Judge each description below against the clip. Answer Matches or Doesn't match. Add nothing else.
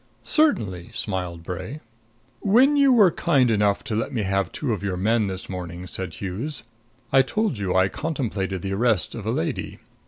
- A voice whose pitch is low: Matches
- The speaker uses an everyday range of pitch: Doesn't match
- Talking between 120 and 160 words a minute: Doesn't match